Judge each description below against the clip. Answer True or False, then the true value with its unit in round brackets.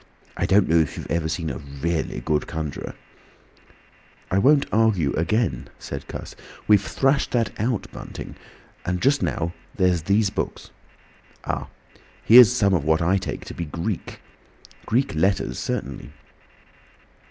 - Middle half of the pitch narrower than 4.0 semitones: False (5.6 semitones)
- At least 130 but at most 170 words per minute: True (140 wpm)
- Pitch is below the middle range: True (95 Hz)